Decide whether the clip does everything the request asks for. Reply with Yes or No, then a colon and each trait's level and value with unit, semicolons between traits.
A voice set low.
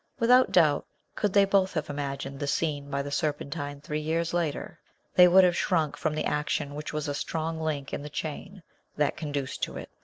No: medium, 150 Hz